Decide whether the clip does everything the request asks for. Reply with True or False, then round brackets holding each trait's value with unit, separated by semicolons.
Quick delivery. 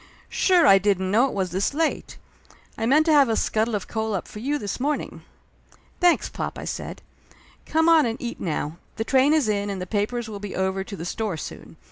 True (225 wpm)